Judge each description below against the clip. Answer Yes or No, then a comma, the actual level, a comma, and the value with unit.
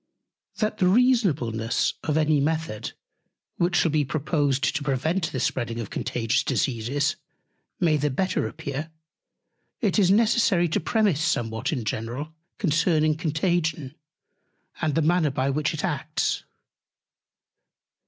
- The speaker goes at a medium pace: No, slow, 125 wpm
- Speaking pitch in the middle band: Yes, medium, 155 Hz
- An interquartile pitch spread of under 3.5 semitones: No, average, 4.3 semitones